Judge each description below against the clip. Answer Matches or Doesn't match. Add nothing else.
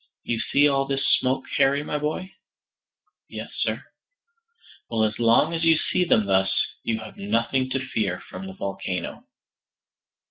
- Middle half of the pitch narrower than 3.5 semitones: Doesn't match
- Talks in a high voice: Doesn't match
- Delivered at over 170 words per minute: Doesn't match